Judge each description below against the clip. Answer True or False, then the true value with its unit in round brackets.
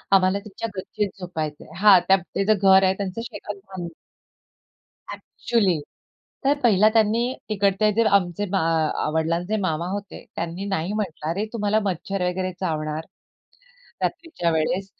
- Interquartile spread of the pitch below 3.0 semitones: False (3.3 semitones)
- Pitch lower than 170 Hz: False (190 Hz)